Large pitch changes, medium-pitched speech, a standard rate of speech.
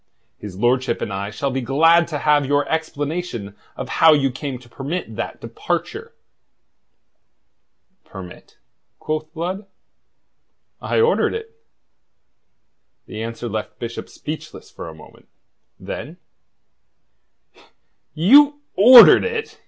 No: wide, 6.6 semitones; medium, 145 Hz; slow, 115 wpm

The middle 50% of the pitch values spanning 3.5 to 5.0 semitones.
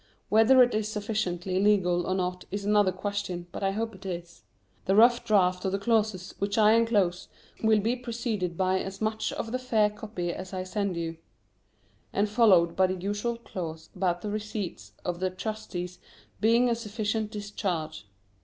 No: average, 3.1 semitones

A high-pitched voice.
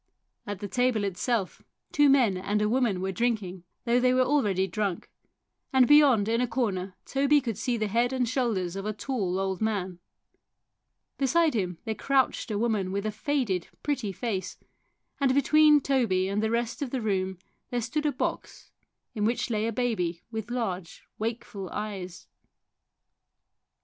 Yes: high, 220 Hz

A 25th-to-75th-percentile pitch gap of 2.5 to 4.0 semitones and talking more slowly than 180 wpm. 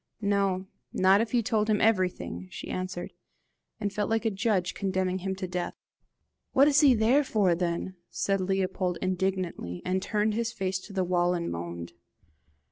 Yes: average, 2.8 semitones; average, 170 wpm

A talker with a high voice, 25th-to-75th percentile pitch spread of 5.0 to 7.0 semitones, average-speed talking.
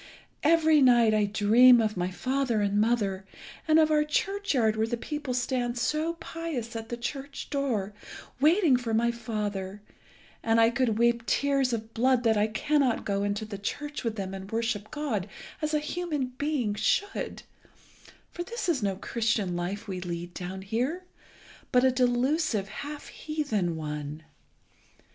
Yes: high, 235 Hz; wide, 5.6 semitones; average, 160 wpm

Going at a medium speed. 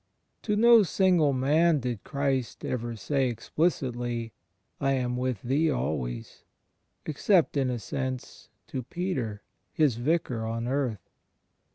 No: slow, 125 wpm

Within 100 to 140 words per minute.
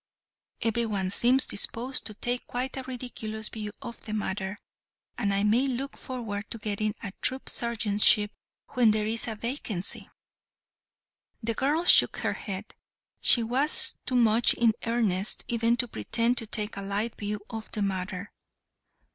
No: average, 155 wpm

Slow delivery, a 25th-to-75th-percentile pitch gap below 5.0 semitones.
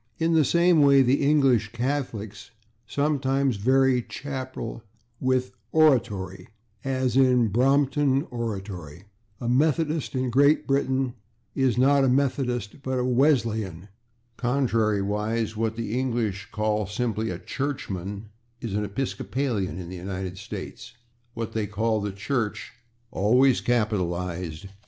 Yes: slow, 125 wpm; average, 4.5 semitones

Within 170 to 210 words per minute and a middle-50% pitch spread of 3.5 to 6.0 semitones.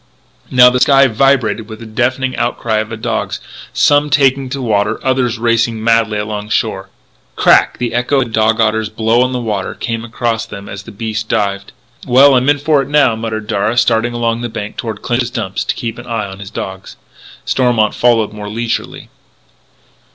No: average, 195 wpm; narrow, 2.4 semitones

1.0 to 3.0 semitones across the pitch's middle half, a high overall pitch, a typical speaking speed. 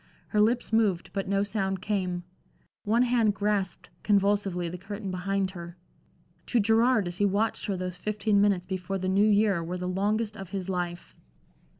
Yes: narrow, 2.4 semitones; high, 195 Hz; average, 175 wpm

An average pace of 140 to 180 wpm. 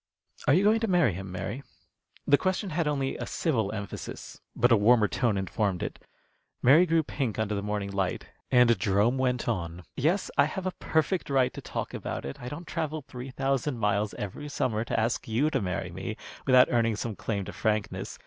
No: average, 200 wpm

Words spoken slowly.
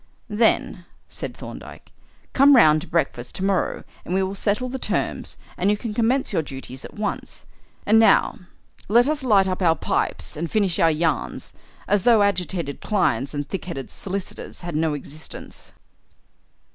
No: average, 160 wpm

